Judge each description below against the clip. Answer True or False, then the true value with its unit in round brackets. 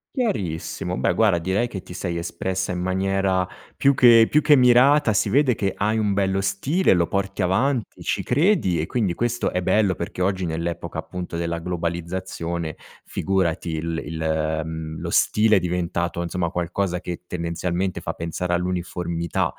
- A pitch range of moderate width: True (3.2 semitones)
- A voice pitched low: True (90 Hz)